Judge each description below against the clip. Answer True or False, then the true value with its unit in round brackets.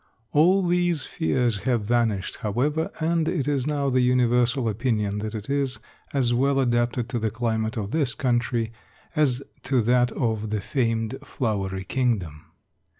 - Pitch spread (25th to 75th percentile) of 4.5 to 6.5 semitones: False (3.6 semitones)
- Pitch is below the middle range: True (120 Hz)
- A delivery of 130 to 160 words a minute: True (150 wpm)